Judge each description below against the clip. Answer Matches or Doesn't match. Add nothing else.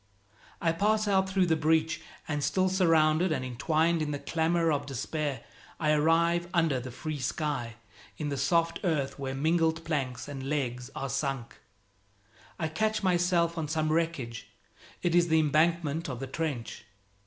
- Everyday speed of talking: Matches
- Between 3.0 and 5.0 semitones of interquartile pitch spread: Matches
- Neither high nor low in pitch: Matches